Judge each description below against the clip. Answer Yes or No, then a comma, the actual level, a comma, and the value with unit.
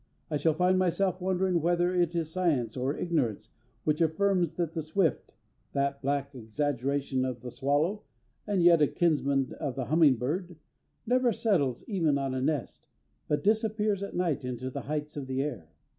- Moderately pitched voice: Yes, medium, 155 Hz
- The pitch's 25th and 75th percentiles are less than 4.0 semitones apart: No, average, 4.7 semitones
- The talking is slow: No, average, 175 wpm